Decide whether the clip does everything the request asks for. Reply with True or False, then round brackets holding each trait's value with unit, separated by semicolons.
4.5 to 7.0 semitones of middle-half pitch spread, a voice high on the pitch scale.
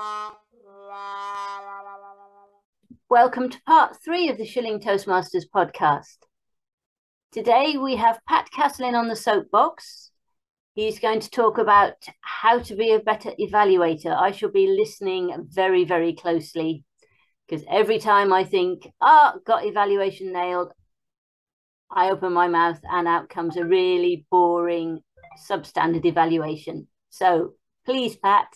True (5.1 semitones; 200 Hz)